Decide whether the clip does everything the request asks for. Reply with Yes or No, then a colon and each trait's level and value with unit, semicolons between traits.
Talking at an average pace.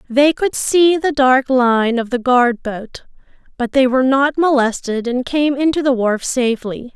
Yes: average, 180 wpm